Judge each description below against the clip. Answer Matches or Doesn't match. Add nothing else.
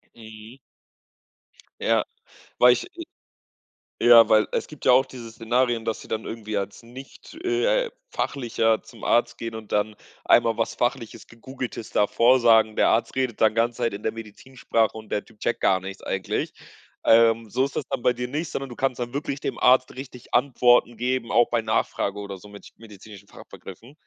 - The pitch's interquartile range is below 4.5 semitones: Matches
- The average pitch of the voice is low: Matches